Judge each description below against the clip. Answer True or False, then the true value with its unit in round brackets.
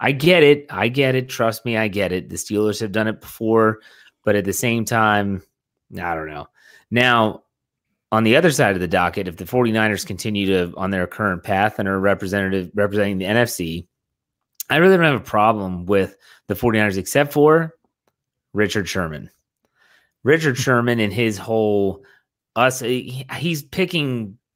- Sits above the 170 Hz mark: False (110 Hz)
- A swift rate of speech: False (170 wpm)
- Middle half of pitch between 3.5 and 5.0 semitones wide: True (4.2 semitones)